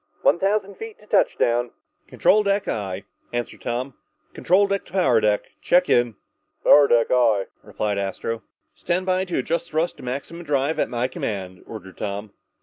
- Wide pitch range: Yes, wide, 8.7 semitones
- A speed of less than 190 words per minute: Yes, average, 165 wpm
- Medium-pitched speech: No, low, 125 Hz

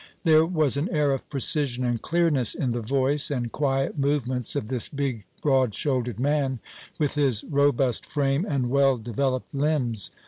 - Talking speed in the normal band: Yes, average, 165 wpm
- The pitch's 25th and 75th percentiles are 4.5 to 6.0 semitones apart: No, average, 2.8 semitones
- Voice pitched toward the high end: No, low, 135 Hz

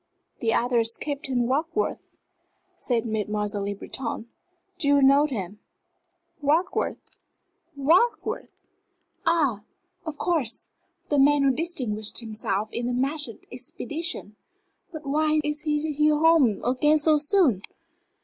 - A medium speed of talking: No, slow, 115 wpm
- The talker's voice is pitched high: Yes, very high, 275 Hz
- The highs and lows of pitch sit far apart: No, average, 4.9 semitones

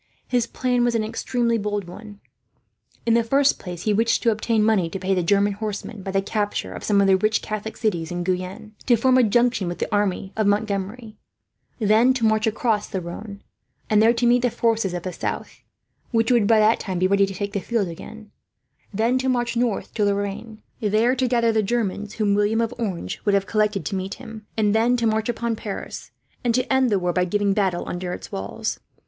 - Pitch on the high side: Yes, high, 215 Hz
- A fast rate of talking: Yes, fast, 225 wpm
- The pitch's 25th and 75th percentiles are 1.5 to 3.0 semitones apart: Yes, average, 2.7 semitones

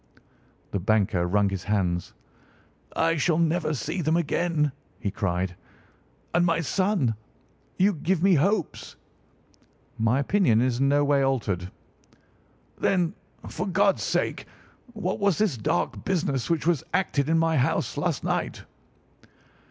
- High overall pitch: No, medium, 150 Hz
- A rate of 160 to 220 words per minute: No, slow, 135 wpm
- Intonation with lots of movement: Yes, wide, 7.7 semitones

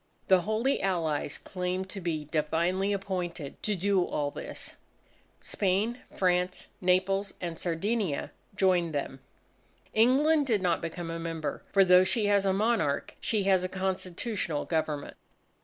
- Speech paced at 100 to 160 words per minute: Yes, average, 140 wpm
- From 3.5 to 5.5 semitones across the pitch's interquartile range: No, average, 3.1 semitones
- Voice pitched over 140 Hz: Yes, medium, 185 Hz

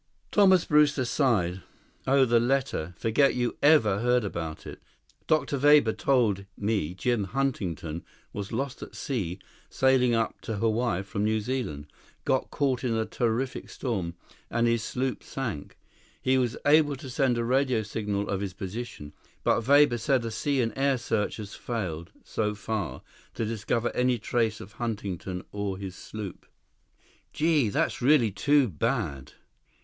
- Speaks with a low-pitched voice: Yes, low, 115 Hz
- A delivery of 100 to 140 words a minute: No, average, 155 wpm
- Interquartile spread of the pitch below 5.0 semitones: Yes, average, 4.5 semitones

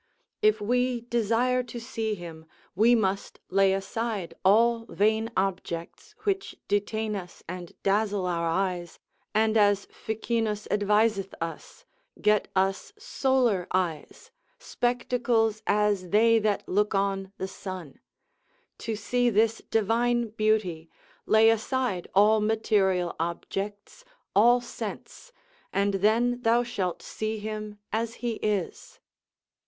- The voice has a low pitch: No, high, 215 Hz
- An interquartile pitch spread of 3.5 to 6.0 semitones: No, average, 3.0 semitones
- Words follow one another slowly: Yes, slow, 115 wpm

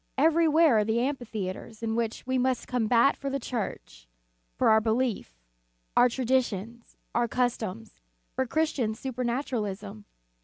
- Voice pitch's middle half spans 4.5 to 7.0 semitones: No, average, 3.1 semitones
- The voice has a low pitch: No, high, 235 Hz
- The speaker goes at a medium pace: No, slow, 130 wpm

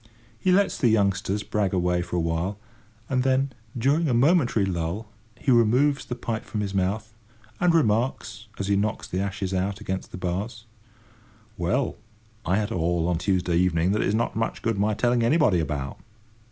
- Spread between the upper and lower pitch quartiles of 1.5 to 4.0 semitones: No, average, 4.5 semitones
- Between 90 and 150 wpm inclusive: No, average, 180 wpm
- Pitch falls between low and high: No, low, 105 Hz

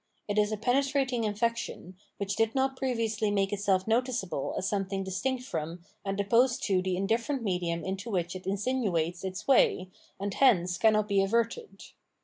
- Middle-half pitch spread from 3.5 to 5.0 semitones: Yes, average, 3.8 semitones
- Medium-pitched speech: No, high, 205 Hz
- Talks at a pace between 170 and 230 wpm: No, average, 160 wpm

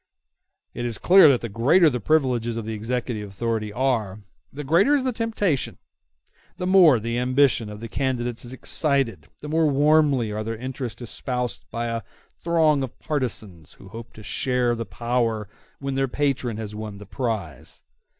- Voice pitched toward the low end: Yes, low, 125 Hz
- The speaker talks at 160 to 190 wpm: Yes, average, 170 wpm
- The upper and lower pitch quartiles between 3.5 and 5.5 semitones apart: Yes, average, 4.0 semitones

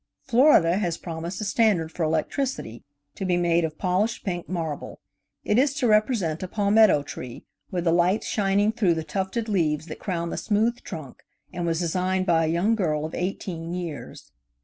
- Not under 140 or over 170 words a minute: No, average, 180 wpm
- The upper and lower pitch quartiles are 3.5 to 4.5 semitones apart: Yes, average, 4.1 semitones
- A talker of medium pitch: Yes, medium, 180 Hz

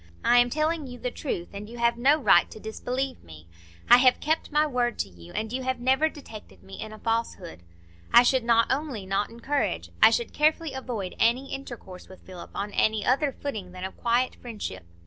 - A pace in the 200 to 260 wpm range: Yes, fast, 205 wpm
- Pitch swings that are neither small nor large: Yes, average, 4.7 semitones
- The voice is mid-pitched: No, high, 235 Hz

